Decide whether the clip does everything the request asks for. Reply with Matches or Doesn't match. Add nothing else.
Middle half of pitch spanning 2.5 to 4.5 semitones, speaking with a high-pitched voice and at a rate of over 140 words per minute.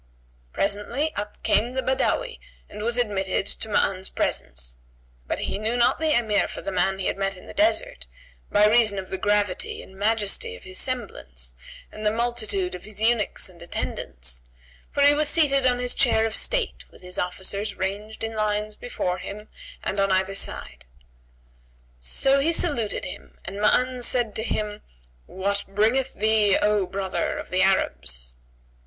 Matches